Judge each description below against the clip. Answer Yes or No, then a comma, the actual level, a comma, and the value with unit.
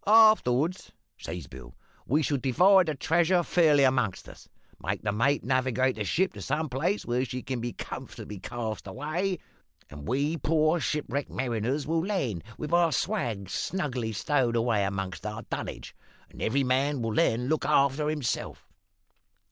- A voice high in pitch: No, low, 135 Hz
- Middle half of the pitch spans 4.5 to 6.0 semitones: Yes, average, 5.3 semitones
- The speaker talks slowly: No, average, 155 wpm